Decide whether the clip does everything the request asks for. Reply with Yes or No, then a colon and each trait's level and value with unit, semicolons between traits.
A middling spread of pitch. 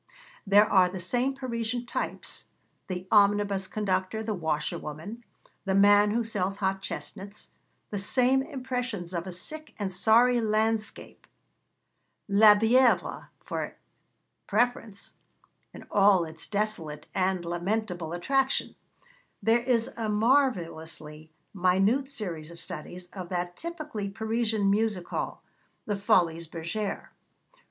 Yes: average, 3.9 semitones